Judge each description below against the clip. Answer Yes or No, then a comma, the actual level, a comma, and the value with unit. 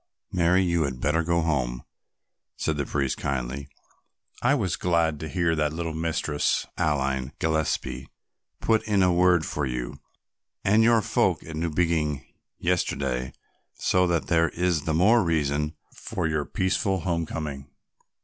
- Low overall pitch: Yes, very low, 80 Hz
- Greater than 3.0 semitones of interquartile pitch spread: Yes, average, 3.6 semitones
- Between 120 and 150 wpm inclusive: Yes, average, 140 wpm